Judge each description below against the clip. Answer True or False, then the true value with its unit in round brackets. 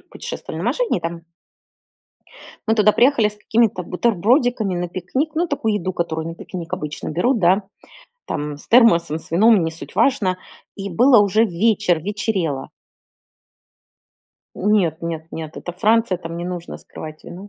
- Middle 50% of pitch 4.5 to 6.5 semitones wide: True (4.9 semitones)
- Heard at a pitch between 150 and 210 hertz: True (185 Hz)